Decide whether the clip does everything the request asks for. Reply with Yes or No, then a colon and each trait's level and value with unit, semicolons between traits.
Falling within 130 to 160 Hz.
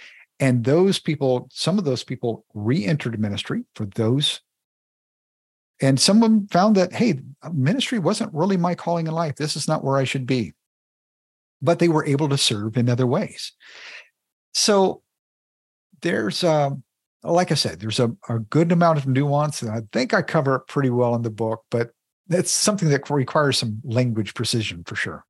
Yes: medium, 140 Hz